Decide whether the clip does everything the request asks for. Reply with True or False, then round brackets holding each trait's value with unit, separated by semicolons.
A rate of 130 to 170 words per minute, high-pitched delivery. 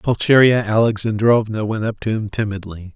False (140 wpm; 110 Hz)